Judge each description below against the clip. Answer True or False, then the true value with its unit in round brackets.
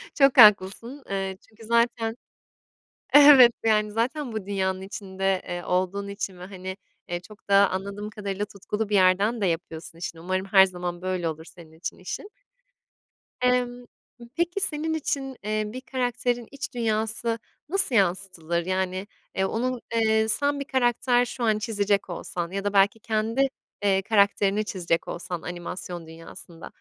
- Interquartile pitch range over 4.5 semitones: False (4.0 semitones)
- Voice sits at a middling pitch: False (205 Hz)